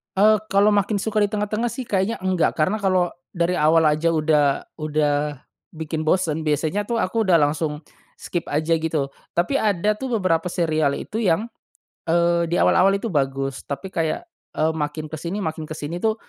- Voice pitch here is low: No, medium, 170 Hz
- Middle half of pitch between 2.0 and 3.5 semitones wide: No, average, 4.4 semitones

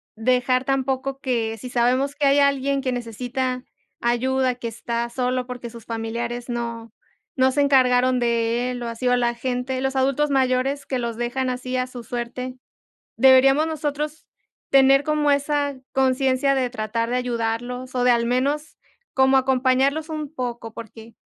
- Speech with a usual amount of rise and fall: No, narrow, 2.1 semitones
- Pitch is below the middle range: No, very high, 255 Hz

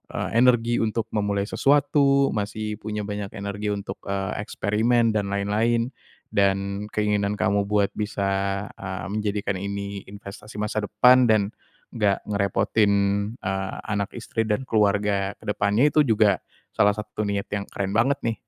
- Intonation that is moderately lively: No, narrow, 1.8 semitones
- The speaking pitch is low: Yes, low, 105 Hz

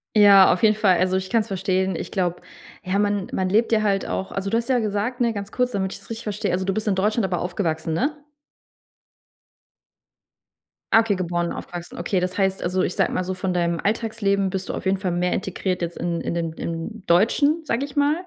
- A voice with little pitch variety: No, average, 3.0 semitones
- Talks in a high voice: Yes, high, 195 Hz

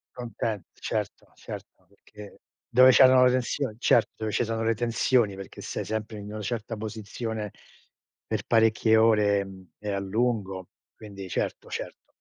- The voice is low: Yes, low, 110 Hz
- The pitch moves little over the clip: Yes, narrow, 2.3 semitones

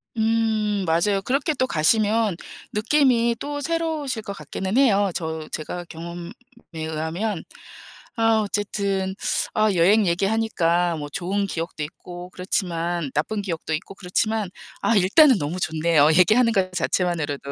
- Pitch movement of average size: Yes, average, 4.7 semitones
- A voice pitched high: Yes, high, 195 Hz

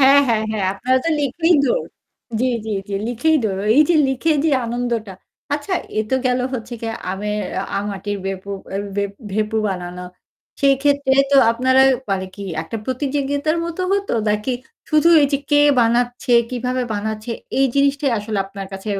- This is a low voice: No, high, 245 Hz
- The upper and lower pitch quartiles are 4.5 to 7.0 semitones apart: Yes, average, 5.2 semitones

